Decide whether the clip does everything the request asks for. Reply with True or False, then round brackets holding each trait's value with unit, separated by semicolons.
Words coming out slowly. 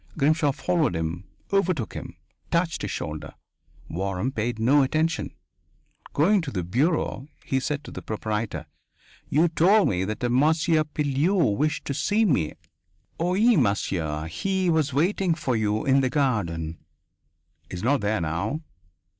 False (145 wpm)